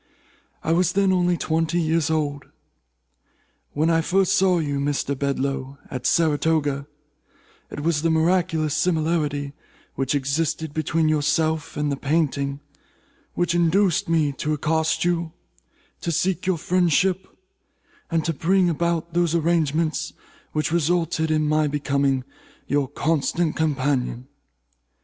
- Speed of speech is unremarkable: No, slow, 125 wpm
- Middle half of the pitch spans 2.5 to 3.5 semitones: Yes, average, 2.8 semitones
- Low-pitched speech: No, medium, 160 Hz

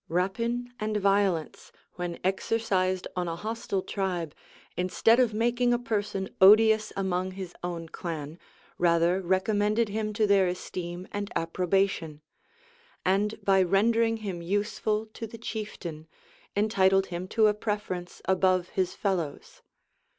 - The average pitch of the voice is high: Yes, high, 195 Hz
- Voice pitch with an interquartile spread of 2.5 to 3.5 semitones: Yes, average, 3.1 semitones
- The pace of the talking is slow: Yes, slow, 130 wpm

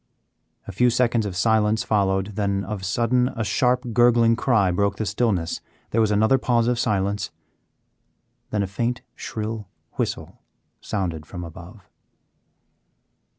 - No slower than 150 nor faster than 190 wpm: No, slow, 135 wpm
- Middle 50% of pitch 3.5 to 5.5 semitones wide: No, average, 3.1 semitones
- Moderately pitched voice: No, low, 105 Hz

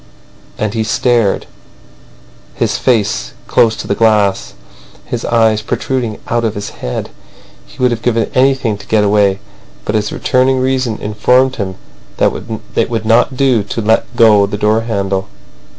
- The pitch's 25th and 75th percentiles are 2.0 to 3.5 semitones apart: Yes, average, 2.7 semitones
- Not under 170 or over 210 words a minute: No, average, 155 wpm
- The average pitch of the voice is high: No, low, 110 Hz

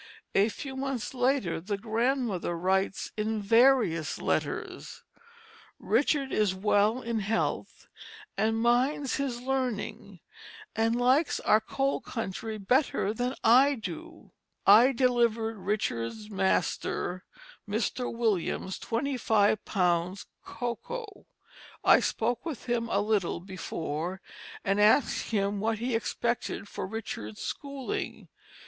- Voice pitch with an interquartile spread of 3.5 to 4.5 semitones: Yes, average, 4.1 semitones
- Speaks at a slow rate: Yes, slow, 110 wpm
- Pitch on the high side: Yes, high, 225 Hz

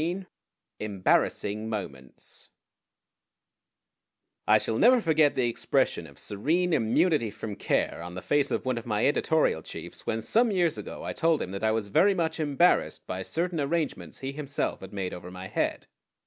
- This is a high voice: No, low, 130 Hz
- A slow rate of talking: No, average, 170 wpm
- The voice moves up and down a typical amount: No, wide, 8.2 semitones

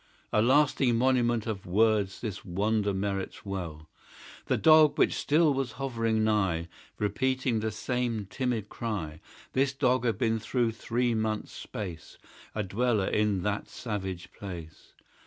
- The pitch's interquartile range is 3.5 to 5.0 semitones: Yes, average, 4.0 semitones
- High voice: No, low, 110 Hz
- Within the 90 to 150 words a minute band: Yes, average, 140 wpm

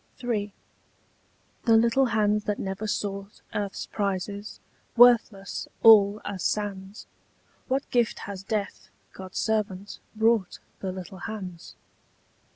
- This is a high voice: Yes, high, 205 Hz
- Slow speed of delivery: Yes, slow, 110 wpm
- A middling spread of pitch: No, narrow, 2.1 semitones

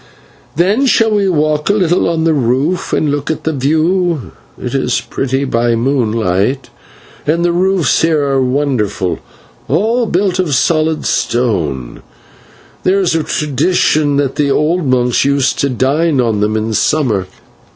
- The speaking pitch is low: No, medium, 145 Hz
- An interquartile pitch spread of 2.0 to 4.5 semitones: No, average, 5.1 semitones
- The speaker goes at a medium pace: Yes, average, 150 wpm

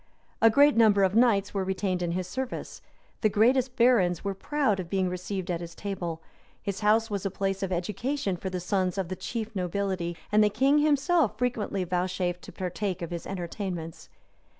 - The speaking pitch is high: Yes, high, 195 Hz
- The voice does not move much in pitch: No, average, 3.6 semitones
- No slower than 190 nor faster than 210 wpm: Yes, average, 195 wpm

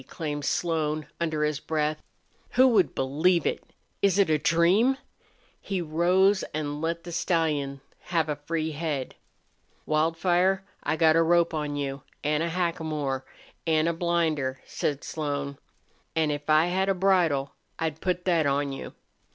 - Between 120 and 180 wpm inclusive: Yes, average, 150 wpm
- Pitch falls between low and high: Yes, medium, 160 Hz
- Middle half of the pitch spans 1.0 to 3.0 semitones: Yes, average, 2.7 semitones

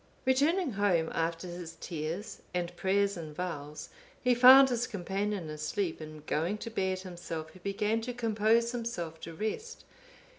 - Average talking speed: Yes, average, 150 wpm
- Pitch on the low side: No, high, 190 Hz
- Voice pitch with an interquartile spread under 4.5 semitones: No, wide, 5.5 semitones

